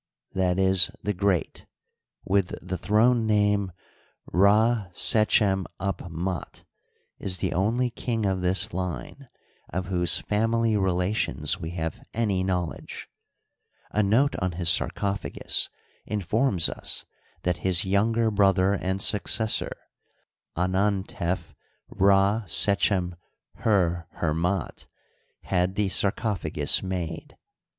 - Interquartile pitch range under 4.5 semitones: Yes, average, 2.7 semitones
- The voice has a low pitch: Yes, very low, 95 Hz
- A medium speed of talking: No, slow, 95 wpm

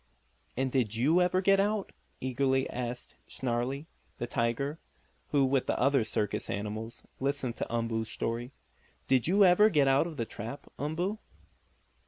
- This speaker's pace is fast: No, average, 150 wpm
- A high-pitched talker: No, low, 135 Hz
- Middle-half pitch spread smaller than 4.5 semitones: No, average, 4.8 semitones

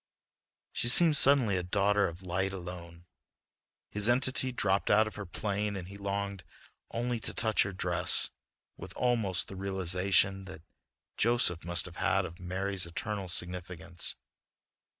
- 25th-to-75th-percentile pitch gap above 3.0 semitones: No, average, 2.7 semitones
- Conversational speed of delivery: Yes, average, 145 wpm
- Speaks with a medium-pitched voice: No, very low, 95 Hz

